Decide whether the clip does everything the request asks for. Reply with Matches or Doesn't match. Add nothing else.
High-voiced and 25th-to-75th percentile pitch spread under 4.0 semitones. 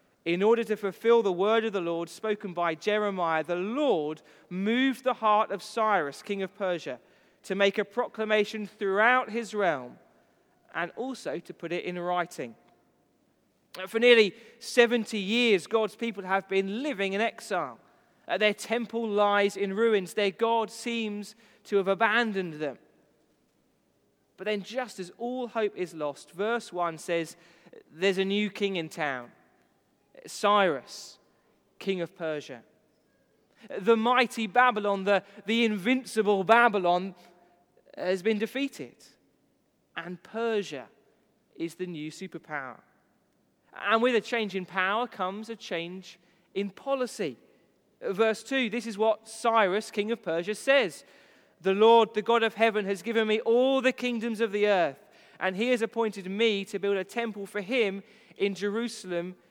Matches